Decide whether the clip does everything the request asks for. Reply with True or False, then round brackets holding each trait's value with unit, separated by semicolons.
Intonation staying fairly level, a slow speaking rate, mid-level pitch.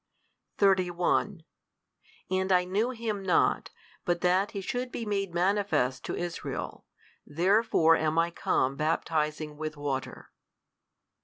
False (4.2 semitones; 120 wpm; 180 Hz)